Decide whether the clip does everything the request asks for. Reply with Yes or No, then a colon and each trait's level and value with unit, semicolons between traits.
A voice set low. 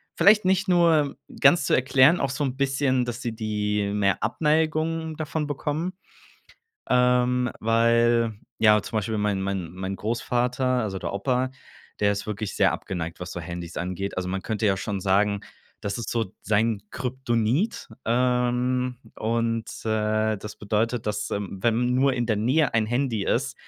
Yes: low, 115 Hz